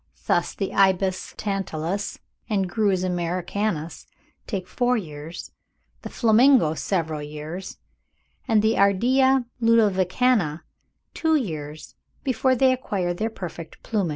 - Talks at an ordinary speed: No, slow, 110 wpm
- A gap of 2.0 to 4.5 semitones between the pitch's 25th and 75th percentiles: No, average, 4.9 semitones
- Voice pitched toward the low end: No, high, 195 Hz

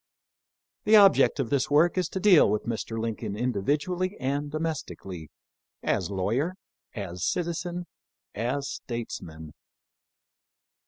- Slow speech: Yes, slow, 115 wpm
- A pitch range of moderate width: No, wide, 8.2 semitones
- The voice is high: No, medium, 140 Hz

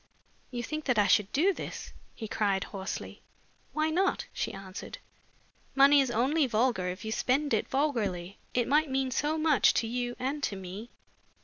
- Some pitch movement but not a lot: No, wide, 5.9 semitones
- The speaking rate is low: No, average, 175 wpm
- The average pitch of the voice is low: No, very high, 250 Hz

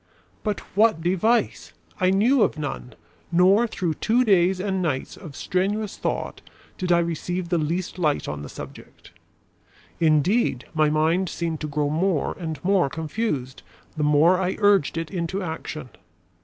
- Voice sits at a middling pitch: Yes, medium, 175 Hz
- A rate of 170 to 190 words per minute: No, average, 155 wpm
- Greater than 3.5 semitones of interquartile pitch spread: Yes, average, 3.9 semitones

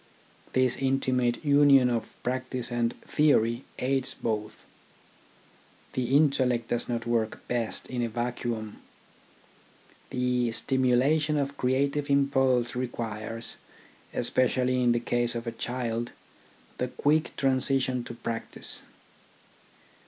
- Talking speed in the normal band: No, slow, 110 wpm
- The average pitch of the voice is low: Yes, low, 125 Hz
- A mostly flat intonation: Yes, narrow, 2.2 semitones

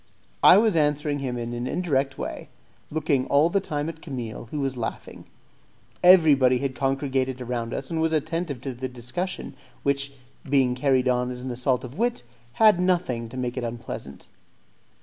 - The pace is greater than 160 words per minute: Yes, average, 170 wpm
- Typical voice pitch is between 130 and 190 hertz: Yes, low, 135 Hz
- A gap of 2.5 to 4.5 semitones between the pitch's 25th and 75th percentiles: Yes, average, 3.9 semitones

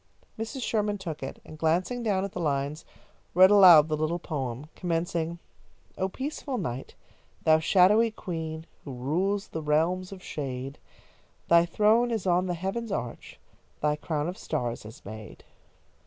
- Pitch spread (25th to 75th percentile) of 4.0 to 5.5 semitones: Yes, average, 4.5 semitones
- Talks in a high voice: No, medium, 170 Hz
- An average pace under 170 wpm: Yes, average, 150 wpm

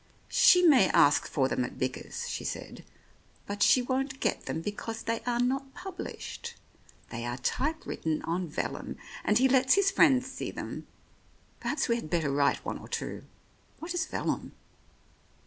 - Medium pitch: No, high, 245 Hz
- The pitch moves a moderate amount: No, wide, 9.0 semitones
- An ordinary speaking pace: Yes, average, 165 wpm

